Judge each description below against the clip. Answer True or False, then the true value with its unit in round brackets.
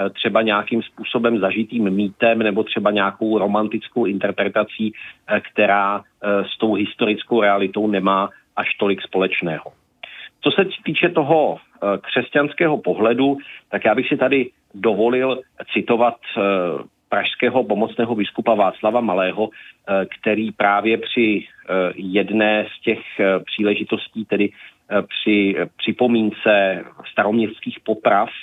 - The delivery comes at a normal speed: False (105 wpm)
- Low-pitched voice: True (105 Hz)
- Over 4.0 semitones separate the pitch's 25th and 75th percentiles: False (2.6 semitones)